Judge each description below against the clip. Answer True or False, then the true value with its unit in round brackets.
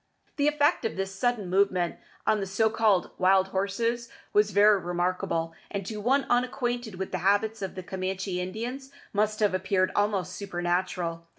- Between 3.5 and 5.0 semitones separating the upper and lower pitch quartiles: False (3.0 semitones)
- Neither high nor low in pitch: False (195 Hz)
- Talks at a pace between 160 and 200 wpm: True (165 wpm)